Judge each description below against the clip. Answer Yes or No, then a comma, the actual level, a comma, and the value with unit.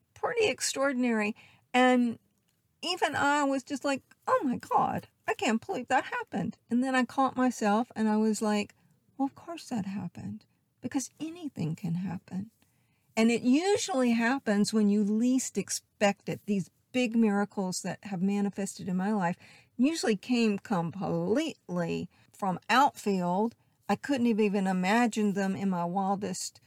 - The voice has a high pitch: Yes, high, 215 Hz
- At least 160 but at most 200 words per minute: No, average, 150 wpm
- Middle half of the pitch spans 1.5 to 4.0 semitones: No, average, 4.6 semitones